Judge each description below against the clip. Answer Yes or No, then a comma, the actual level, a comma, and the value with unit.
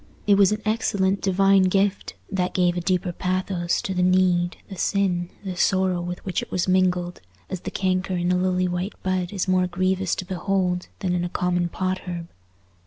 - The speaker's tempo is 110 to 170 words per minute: No, average, 195 wpm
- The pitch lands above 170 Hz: Yes, medium, 185 Hz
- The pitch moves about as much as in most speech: No, narrow, 1.2 semitones